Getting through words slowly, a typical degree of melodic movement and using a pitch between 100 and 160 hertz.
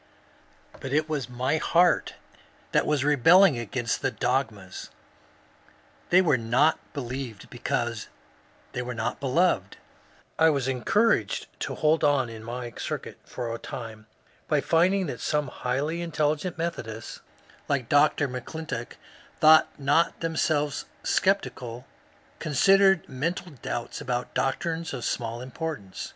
Yes: slow, 125 wpm; average, 4.8 semitones; medium, 140 Hz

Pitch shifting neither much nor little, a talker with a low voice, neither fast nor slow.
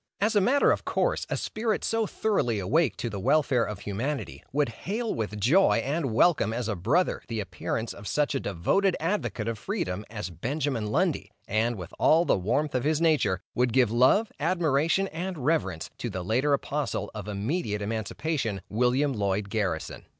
No: wide, 7.2 semitones; low, 125 Hz; average, 180 wpm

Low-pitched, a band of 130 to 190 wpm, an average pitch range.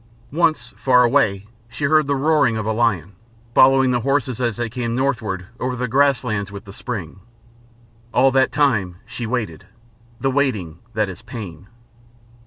Yes: low, 120 Hz; average, 165 wpm; average, 4.2 semitones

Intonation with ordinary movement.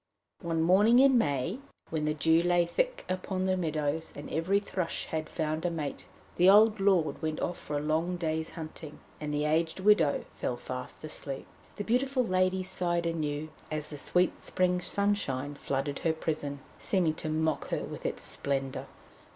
Yes: average, 3.4 semitones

